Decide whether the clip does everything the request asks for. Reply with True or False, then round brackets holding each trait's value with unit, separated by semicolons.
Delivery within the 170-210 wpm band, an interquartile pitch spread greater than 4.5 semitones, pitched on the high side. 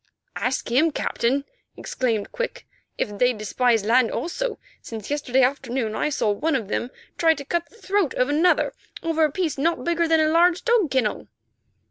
True (175 wpm; 5.5 semitones; 285 Hz)